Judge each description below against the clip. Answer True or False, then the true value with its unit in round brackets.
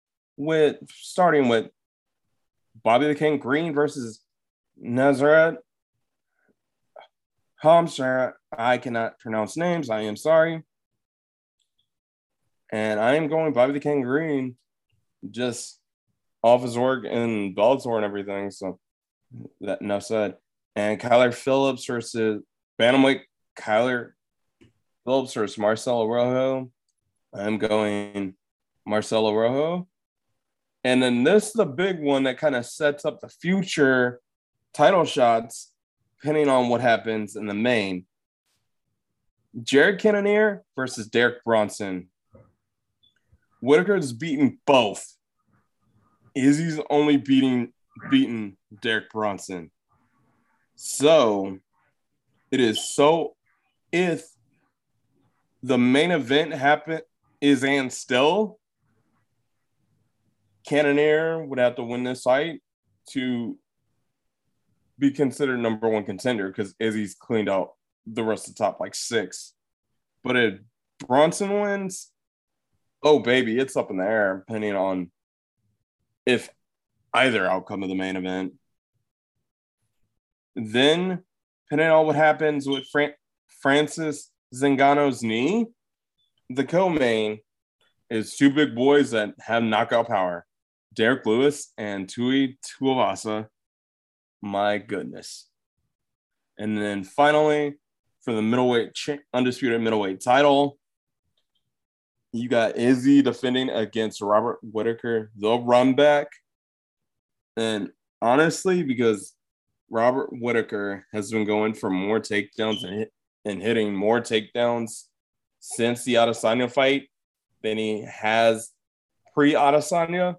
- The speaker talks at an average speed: False (110 wpm)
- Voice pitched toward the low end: True (120 Hz)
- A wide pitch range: False (5.0 semitones)